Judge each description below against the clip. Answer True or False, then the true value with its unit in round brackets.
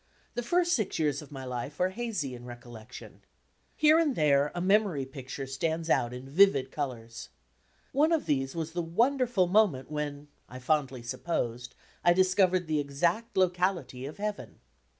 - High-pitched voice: False (155 Hz)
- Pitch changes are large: True (6.3 semitones)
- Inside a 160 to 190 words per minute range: True (165 wpm)